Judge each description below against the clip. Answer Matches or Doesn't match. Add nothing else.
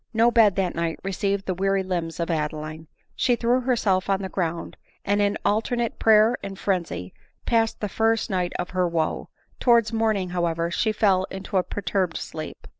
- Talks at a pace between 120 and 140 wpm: Doesn't match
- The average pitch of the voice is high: Matches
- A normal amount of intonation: Matches